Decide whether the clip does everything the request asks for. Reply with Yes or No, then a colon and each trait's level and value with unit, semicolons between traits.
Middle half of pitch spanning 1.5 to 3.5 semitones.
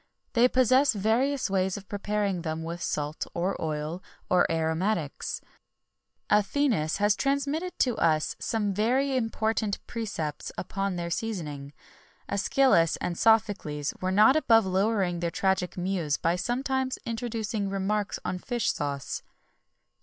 No: average, 5.0 semitones